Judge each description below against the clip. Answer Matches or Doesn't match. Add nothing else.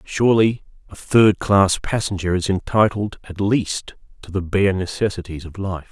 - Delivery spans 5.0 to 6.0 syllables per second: Doesn't match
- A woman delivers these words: Doesn't match